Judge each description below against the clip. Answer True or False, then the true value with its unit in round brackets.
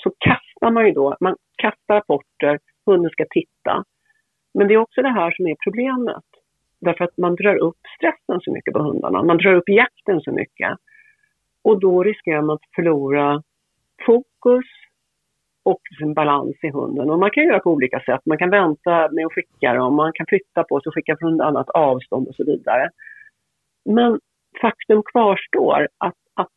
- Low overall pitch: False (185 Hz)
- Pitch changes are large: True (6.2 semitones)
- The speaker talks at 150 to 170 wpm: False (180 wpm)